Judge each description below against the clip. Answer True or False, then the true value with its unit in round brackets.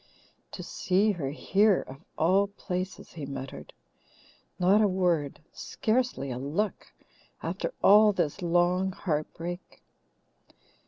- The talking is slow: True (110 wpm)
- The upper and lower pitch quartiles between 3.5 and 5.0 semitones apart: True (4.5 semitones)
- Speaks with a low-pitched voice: False (180 Hz)